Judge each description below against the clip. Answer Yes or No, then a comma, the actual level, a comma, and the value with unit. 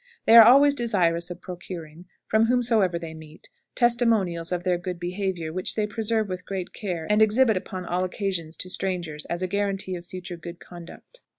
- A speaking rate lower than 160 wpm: No, average, 185 wpm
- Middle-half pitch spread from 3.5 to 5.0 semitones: Yes, average, 3.8 semitones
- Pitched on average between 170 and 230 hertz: Yes, medium, 185 Hz